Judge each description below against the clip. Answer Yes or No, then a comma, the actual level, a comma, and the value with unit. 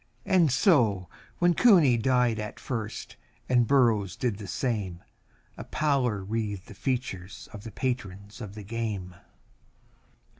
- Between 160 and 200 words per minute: No, slow, 135 wpm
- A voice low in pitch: Yes, low, 115 Hz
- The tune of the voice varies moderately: Yes, average, 4.1 semitones